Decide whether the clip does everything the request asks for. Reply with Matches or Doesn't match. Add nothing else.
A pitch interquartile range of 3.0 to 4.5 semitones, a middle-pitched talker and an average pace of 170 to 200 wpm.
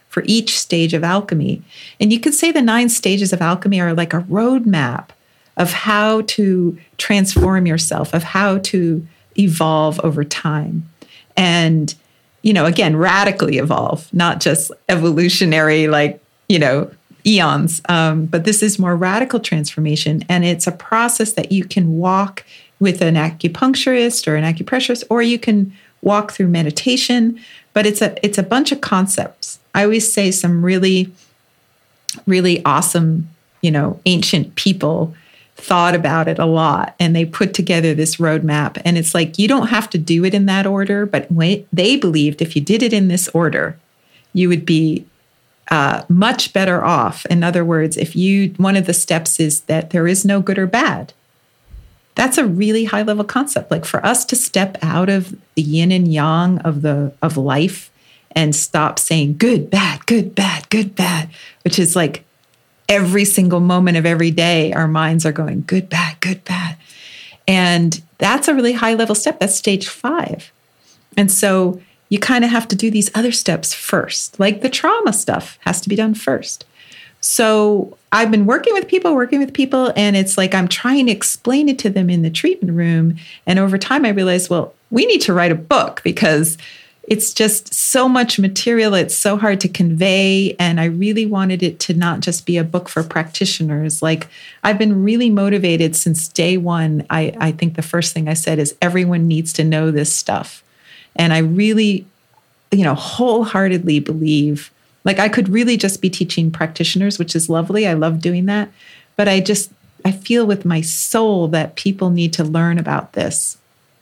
Matches